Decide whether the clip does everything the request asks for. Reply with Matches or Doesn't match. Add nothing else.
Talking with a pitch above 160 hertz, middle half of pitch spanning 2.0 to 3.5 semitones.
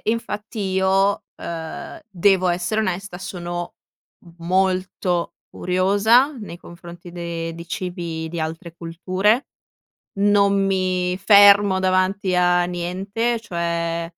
Matches